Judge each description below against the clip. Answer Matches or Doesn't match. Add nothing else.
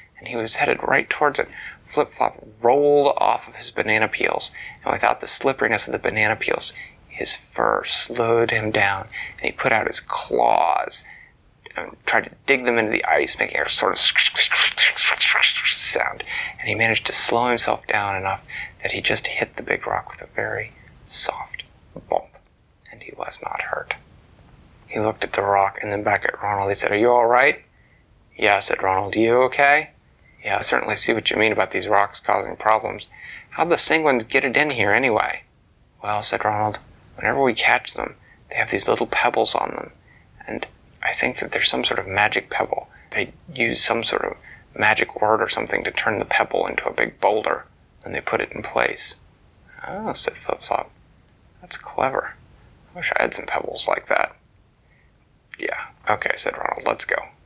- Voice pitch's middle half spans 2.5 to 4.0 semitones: Matches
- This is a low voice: Matches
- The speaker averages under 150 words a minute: Doesn't match